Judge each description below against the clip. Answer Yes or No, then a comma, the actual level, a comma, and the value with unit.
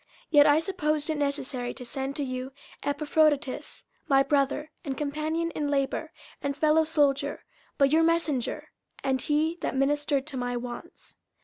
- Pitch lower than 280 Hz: No, very high, 290 Hz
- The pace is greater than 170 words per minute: No, average, 150 wpm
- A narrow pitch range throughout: Yes, narrow, 2.1 semitones